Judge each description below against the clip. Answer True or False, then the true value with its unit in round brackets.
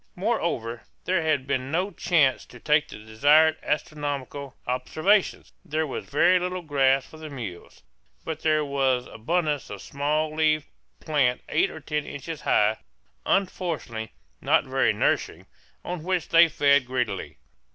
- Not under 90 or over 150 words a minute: True (145 wpm)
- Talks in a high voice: False (150 Hz)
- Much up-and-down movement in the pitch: False (3.4 semitones)